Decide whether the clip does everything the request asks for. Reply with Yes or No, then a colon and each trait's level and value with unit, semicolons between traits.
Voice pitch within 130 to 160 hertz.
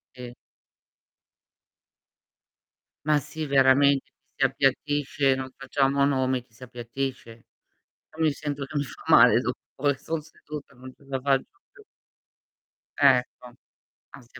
Yes: low, 135 Hz